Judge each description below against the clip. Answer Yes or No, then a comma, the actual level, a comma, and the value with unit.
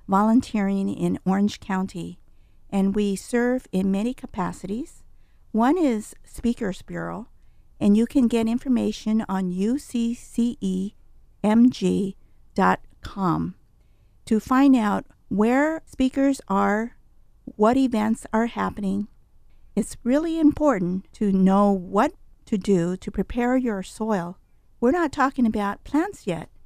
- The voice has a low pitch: No, high, 220 Hz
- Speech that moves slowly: Yes, slow, 110 wpm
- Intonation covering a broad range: No, average, 4.2 semitones